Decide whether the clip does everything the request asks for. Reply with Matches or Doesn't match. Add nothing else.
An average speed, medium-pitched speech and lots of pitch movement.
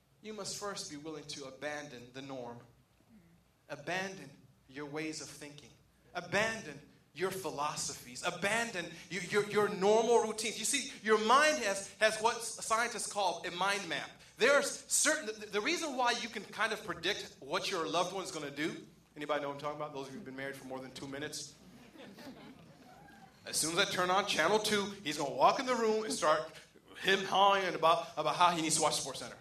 Matches